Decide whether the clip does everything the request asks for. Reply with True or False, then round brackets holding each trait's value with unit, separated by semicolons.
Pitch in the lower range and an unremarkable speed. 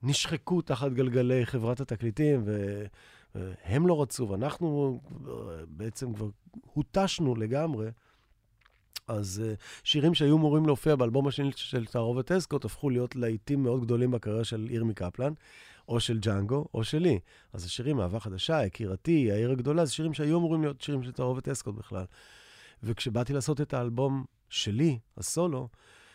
True (125 Hz; 140 wpm)